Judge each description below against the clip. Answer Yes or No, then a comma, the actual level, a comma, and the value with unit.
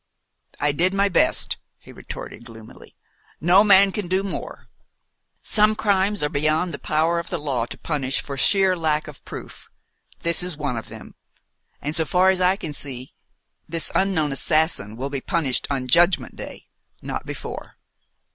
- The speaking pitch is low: No, medium, 160 Hz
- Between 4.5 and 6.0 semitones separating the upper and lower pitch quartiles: Yes, average, 4.8 semitones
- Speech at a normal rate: Yes, average, 165 wpm